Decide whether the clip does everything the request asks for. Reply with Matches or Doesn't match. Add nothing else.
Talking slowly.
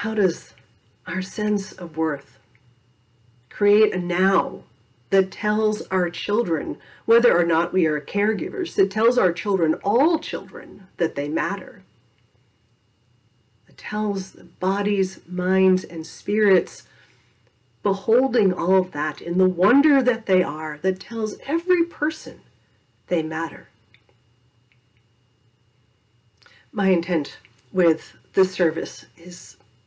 Matches